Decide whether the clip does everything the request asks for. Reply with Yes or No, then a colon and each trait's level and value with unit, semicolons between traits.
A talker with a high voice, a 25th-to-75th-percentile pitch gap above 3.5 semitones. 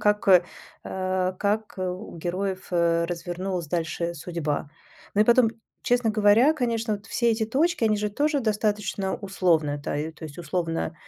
Yes: high, 195 Hz; average, 4.2 semitones